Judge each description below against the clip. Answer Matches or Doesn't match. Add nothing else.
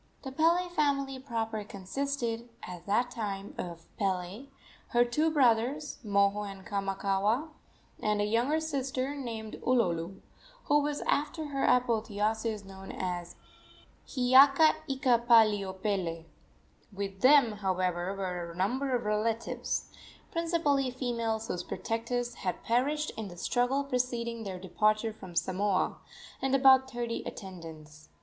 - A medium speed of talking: Doesn't match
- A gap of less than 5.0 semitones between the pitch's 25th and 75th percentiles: Doesn't match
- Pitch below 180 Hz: Doesn't match